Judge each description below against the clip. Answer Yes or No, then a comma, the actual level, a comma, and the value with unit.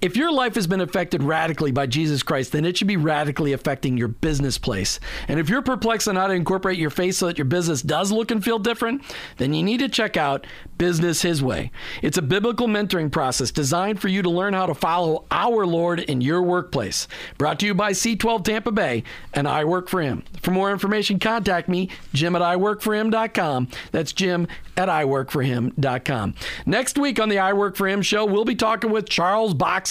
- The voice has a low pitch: No, medium, 180 Hz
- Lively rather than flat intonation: Yes, wide, 5.7 semitones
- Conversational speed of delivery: No, fast, 210 wpm